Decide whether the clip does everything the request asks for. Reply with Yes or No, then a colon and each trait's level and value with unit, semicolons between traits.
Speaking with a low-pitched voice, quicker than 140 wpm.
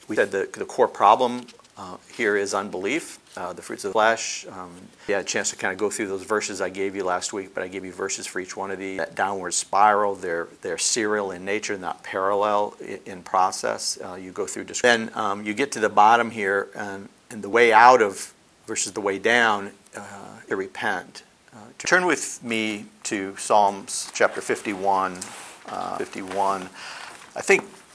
Yes: low, 100 Hz; average, 200 wpm